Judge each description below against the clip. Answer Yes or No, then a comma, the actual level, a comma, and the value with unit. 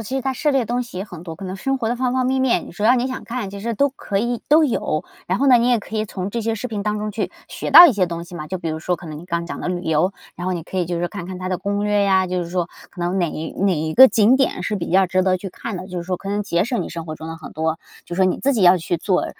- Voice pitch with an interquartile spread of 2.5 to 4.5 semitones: No, average, 4.9 semitones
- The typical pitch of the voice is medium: No, high, 195 Hz